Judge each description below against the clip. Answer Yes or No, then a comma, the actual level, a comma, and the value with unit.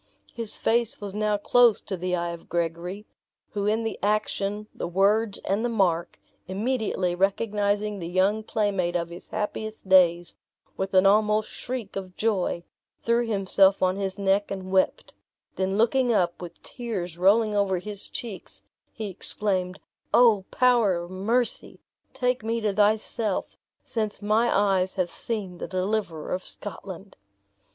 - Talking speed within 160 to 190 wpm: No, average, 150 wpm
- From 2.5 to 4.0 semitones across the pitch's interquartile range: Yes, average, 2.8 semitones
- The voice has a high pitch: Yes, high, 200 Hz